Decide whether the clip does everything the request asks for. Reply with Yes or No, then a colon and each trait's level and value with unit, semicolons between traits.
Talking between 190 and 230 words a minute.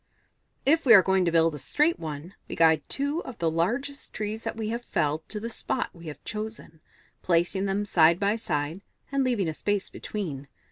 Yes: average, 200 wpm